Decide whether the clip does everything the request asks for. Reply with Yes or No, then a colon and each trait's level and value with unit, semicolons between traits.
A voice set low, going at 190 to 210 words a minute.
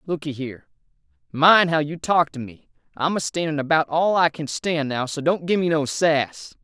No: medium, 155 Hz; average, 200 wpm